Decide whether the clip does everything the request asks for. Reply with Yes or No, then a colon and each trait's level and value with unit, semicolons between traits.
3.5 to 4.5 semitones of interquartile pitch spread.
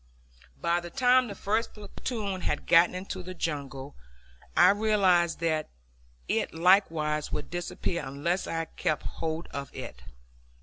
Yes: average, 3.9 semitones